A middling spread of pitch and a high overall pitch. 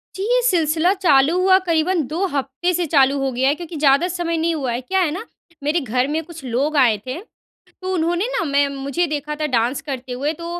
Yes: average, 4.2 semitones; very high, 305 Hz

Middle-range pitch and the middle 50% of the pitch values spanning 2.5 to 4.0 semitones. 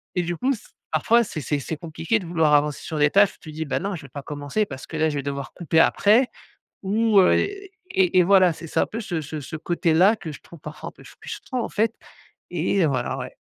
No: medium, 170 Hz; average, 4.9 semitones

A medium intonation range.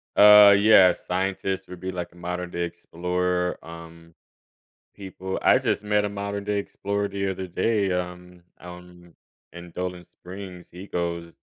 No: narrow, 2.1 semitones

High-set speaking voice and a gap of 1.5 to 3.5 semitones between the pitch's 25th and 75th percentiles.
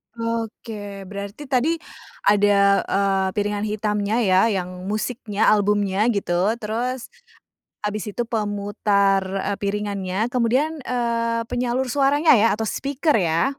Yes: high, 210 Hz; average, 2.9 semitones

